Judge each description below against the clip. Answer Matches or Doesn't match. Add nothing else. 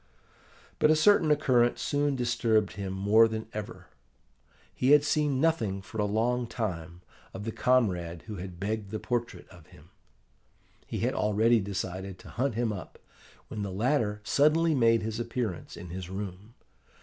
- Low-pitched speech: Matches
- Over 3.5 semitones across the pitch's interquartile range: Matches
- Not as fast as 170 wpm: Matches